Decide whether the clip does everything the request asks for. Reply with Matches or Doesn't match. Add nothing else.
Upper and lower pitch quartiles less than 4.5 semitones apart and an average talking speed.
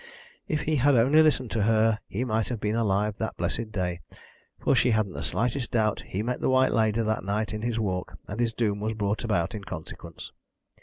Doesn't match